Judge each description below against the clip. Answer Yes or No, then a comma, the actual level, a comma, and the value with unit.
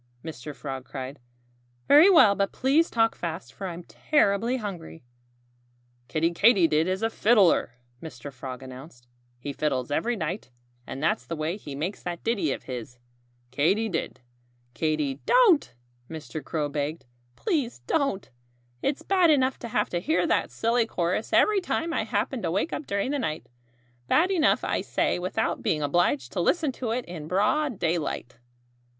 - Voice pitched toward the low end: No, medium, 180 Hz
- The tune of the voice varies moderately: No, wide, 8.2 semitones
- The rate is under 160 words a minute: No, average, 165 wpm